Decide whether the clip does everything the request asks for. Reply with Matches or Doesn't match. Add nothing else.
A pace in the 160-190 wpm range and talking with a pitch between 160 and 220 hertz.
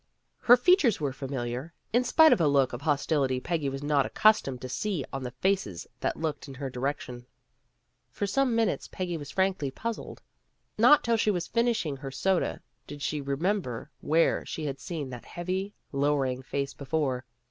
Doesn't match